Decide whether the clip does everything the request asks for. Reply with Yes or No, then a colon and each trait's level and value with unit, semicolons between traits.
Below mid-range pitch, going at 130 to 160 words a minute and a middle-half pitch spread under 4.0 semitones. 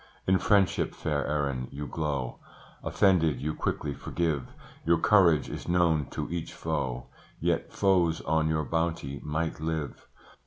Yes: very low, 80 Hz; average, 140 wpm; average, 2.9 semitones